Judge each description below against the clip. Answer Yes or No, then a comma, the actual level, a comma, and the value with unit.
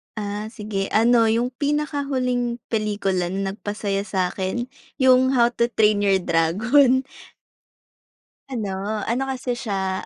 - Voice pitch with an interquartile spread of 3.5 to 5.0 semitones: Yes, average, 4.1 semitones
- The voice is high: Yes, high, 220 Hz